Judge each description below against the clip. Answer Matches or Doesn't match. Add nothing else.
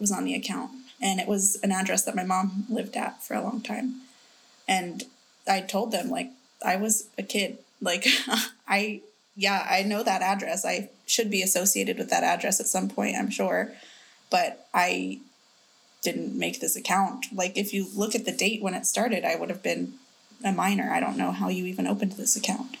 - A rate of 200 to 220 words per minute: Matches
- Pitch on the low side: Doesn't match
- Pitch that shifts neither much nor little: Matches